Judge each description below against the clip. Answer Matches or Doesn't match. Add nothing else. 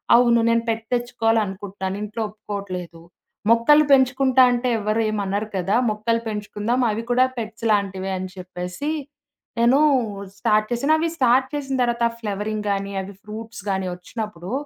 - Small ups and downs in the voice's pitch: Doesn't match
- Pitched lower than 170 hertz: Doesn't match